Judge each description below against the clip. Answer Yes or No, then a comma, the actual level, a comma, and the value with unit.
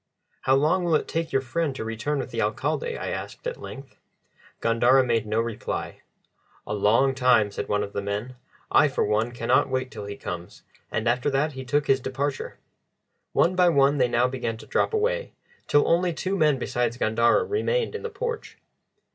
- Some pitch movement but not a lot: No, wide, 5.9 semitones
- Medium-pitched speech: No, low, 130 Hz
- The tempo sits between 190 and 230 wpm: Yes, average, 195 wpm